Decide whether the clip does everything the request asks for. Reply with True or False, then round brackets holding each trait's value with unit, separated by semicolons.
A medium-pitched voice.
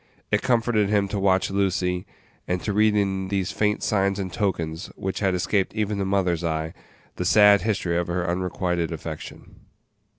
False (95 Hz)